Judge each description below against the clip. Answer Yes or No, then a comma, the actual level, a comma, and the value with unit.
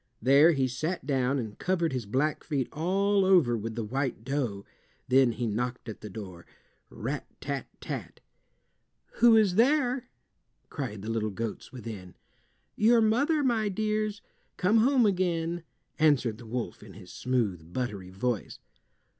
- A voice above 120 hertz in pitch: Yes, low, 135 Hz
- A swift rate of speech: No, average, 145 wpm